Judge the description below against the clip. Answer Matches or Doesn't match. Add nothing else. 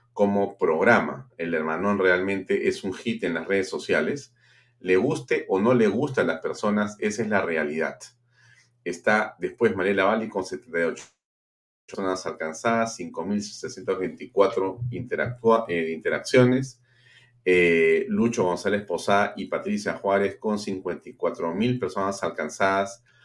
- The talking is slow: Matches